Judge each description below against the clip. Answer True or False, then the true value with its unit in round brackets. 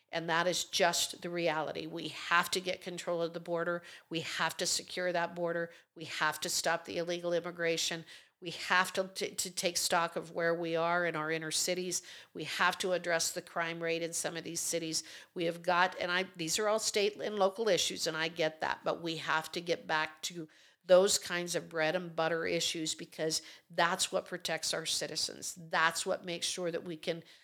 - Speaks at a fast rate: True (210 wpm)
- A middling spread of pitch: False (1.4 semitones)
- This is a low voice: False (170 Hz)